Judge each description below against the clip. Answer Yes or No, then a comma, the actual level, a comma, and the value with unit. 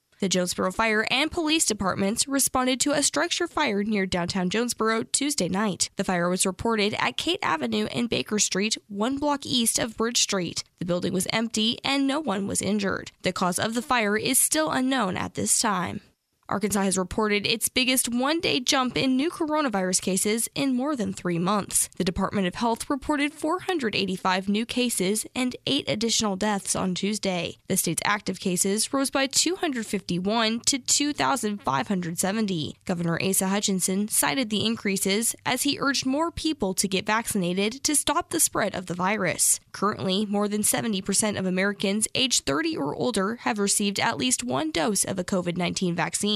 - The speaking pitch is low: No, high, 215 Hz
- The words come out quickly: No, average, 170 wpm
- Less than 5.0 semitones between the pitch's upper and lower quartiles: No, average, 5.3 semitones